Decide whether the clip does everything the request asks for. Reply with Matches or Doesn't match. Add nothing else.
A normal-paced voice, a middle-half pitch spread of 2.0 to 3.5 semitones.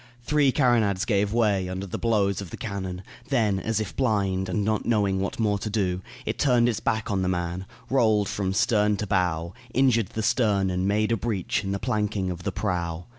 Doesn't match